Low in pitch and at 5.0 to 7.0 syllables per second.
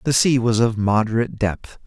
Yes: low, 115 Hz; 5.3 syllables/s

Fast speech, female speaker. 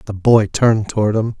No: fast, 215 wpm; male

